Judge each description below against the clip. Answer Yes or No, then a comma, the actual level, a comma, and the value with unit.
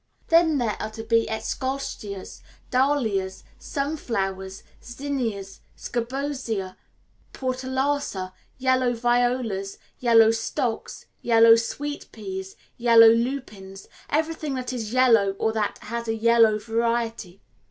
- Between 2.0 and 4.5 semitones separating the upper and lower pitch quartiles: Yes, average, 3.4 semitones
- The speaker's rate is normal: No, slow, 100 wpm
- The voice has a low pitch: No, high, 230 Hz